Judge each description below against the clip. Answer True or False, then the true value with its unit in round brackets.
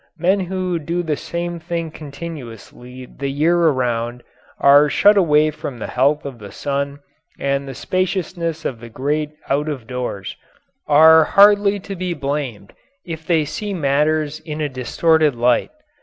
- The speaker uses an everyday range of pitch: True (3.7 semitones)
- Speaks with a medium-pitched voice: True (150 Hz)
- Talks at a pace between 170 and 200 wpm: False (155 wpm)